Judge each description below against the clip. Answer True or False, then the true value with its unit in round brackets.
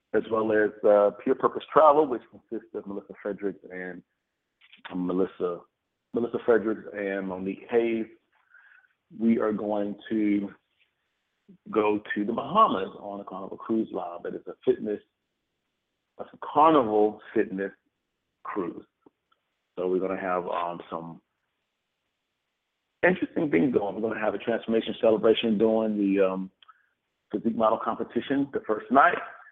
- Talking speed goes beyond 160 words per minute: False (135 wpm)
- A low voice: True (105 Hz)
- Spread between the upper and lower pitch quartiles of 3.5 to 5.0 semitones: False (2.7 semitones)